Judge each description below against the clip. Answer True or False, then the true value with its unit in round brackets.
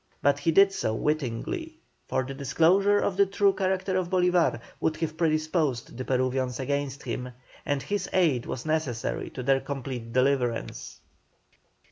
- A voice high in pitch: False (150 Hz)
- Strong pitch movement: True (6.1 semitones)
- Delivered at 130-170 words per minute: True (150 wpm)